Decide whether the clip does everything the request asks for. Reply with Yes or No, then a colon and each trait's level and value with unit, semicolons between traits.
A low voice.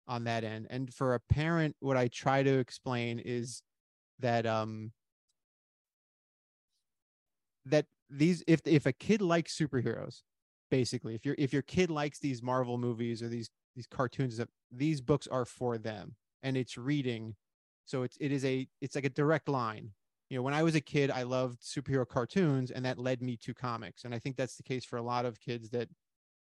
Yes: low, 125 Hz